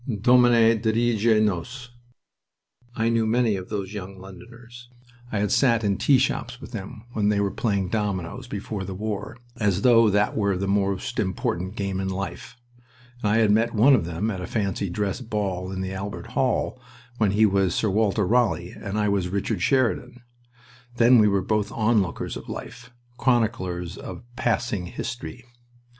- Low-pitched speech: Yes, low, 105 Hz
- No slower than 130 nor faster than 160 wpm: No, average, 170 wpm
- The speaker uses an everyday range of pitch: Yes, average, 3.2 semitones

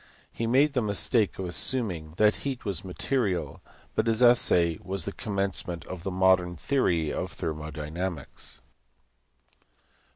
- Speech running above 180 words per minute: No, slow, 135 wpm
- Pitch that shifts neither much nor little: Yes, average, 4.7 semitones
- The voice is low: Yes, very low, 95 Hz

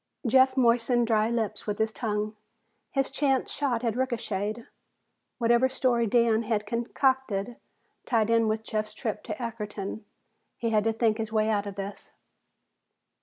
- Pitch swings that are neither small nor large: No, narrow, 2.0 semitones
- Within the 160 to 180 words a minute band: No, average, 150 wpm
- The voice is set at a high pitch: Yes, high, 225 Hz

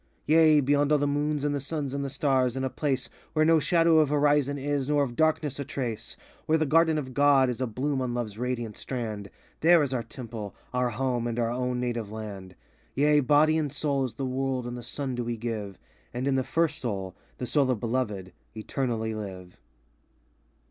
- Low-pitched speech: Yes, low, 130 Hz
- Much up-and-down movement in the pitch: No, average, 3.6 semitones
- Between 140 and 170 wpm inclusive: No, fast, 205 wpm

